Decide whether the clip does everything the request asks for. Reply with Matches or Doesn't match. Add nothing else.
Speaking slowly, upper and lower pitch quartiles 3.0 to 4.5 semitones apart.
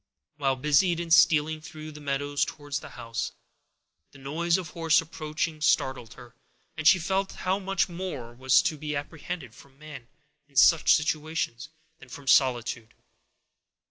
Doesn't match